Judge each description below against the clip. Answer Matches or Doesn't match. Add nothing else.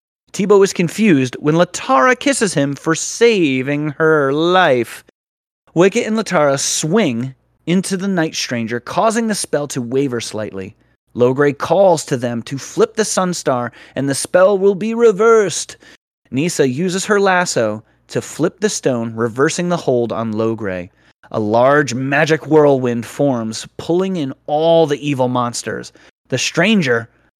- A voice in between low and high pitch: Matches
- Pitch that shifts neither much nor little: Doesn't match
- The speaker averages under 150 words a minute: Matches